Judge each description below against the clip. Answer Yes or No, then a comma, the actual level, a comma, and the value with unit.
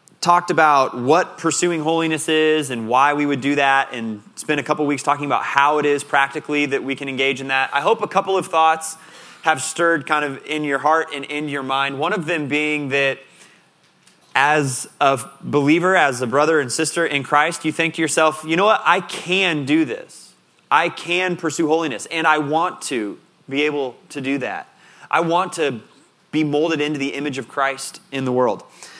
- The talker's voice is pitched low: No, medium, 150 Hz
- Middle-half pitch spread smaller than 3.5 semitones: Yes, average, 2.8 semitones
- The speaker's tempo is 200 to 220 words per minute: Yes, fast, 205 wpm